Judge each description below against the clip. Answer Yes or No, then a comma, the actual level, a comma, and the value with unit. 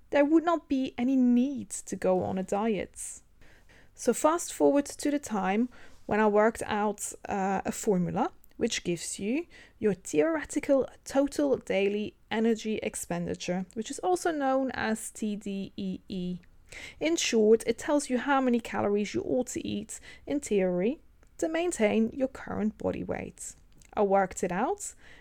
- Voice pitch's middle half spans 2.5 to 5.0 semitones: No, wide, 5.5 semitones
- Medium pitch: No, high, 225 Hz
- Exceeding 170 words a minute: No, average, 150 wpm